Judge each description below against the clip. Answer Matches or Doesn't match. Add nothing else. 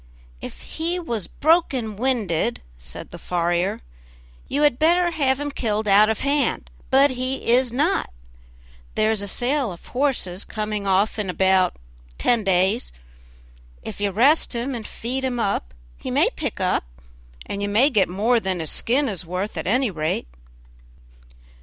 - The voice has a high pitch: Matches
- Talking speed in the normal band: Matches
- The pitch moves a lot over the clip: Matches